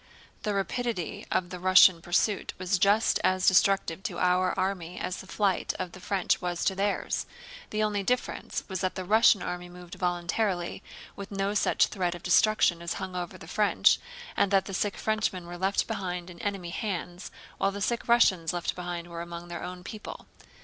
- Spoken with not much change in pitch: Yes, narrow, 2.2 semitones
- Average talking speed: Yes, average, 190 wpm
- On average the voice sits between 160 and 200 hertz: Yes, medium, 185 Hz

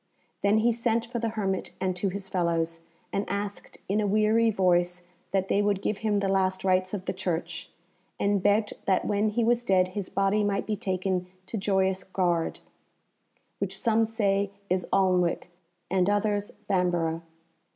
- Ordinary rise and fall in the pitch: No, narrow, 2.2 semitones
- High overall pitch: Yes, high, 195 Hz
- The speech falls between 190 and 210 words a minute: No, average, 170 wpm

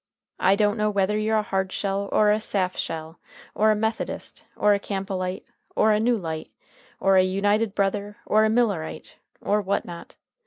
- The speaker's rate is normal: Yes, average, 170 wpm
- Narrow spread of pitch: Yes, narrow, 2.0 semitones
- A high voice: Yes, high, 200 Hz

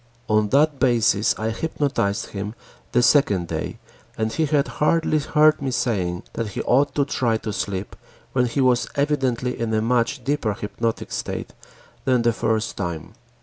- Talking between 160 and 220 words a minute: Yes, average, 165 wpm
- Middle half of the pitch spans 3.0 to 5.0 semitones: Yes, average, 4.6 semitones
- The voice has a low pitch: Yes, low, 120 Hz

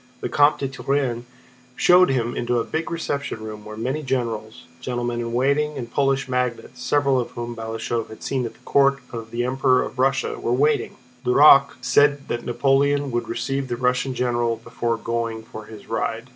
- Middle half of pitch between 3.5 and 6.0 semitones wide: No, average, 2.7 semitones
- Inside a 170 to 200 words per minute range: Yes, average, 175 wpm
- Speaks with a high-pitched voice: No, low, 125 Hz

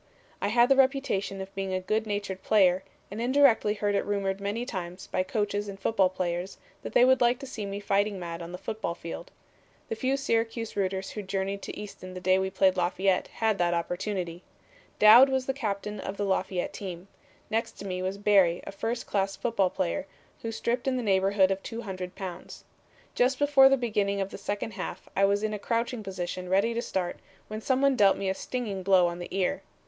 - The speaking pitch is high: Yes, high, 200 Hz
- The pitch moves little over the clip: No, average, 3.2 semitones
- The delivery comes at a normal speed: No, fast, 210 wpm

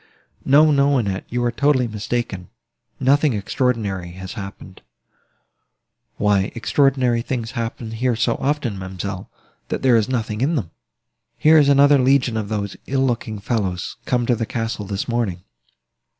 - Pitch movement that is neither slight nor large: Yes, average, 4.5 semitones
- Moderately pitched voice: No, low, 115 Hz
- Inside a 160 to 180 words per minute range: No, average, 150 wpm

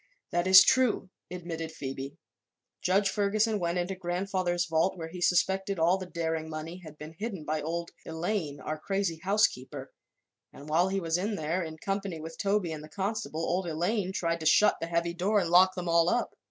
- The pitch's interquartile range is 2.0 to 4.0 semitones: Yes, average, 3.0 semitones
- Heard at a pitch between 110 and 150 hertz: No, medium, 175 Hz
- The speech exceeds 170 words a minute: Yes, average, 195 wpm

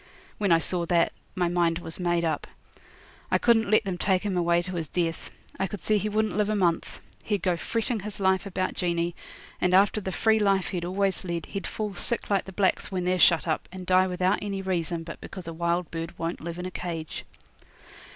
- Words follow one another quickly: Yes, fast, 220 wpm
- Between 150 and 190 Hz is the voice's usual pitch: Yes, medium, 185 Hz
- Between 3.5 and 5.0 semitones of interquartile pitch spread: No, narrow, 2.6 semitones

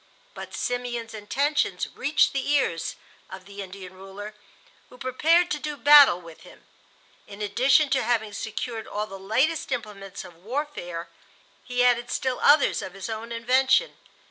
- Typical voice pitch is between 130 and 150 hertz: No, high, 235 Hz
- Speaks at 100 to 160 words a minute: Yes, average, 150 wpm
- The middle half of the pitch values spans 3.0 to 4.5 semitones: No, wide, 5.4 semitones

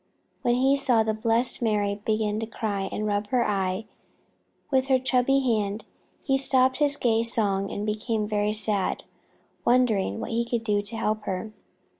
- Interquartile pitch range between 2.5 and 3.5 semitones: Yes, average, 3.0 semitones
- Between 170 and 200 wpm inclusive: Yes, average, 175 wpm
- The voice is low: No, high, 220 Hz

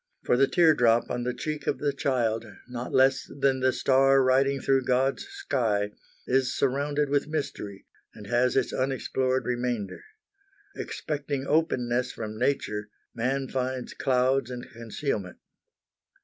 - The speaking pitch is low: Yes, low, 130 Hz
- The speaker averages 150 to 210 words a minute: No, slow, 135 wpm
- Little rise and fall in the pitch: Yes, narrow, 2.2 semitones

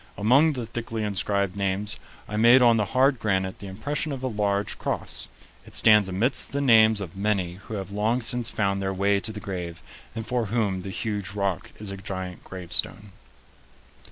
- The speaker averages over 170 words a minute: Yes, average, 185 wpm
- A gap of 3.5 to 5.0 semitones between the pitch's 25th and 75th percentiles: No, average, 2.8 semitones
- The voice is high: No, low, 105 Hz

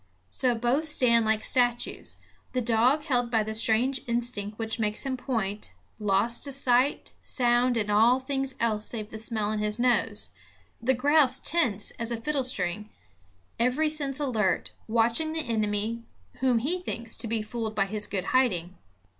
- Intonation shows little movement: No, average, 3.2 semitones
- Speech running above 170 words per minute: No, average, 165 wpm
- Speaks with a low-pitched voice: No, high, 235 Hz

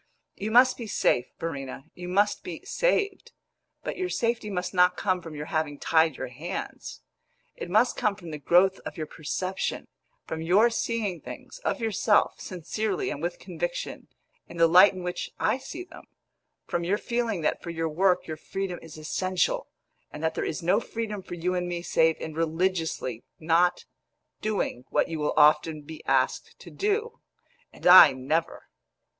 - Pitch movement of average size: Yes, average, 4.8 semitones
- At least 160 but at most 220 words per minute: Yes, average, 175 wpm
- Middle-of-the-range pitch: Yes, medium, 180 Hz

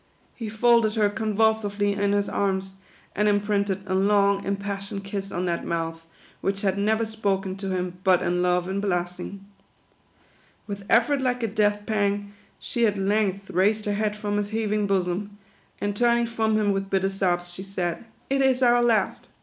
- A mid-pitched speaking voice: No, high, 200 Hz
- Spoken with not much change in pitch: Yes, narrow, 1.9 semitones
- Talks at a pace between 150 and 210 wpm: Yes, average, 175 wpm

